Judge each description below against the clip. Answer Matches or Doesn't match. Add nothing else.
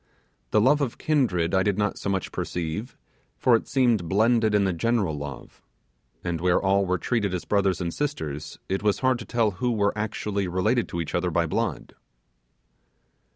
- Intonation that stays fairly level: Doesn't match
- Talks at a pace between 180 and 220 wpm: Matches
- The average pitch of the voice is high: Doesn't match